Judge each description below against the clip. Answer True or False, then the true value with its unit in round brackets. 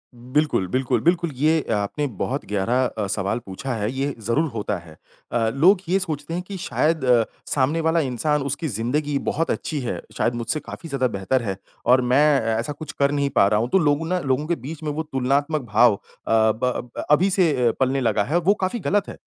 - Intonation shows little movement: False (5.0 semitones)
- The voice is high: False (140 Hz)